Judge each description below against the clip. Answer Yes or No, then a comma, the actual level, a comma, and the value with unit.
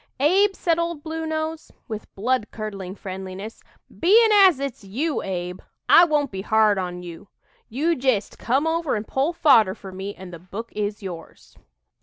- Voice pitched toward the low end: No, high, 225 Hz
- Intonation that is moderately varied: No, wide, 8.6 semitones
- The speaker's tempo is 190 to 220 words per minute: No, average, 165 wpm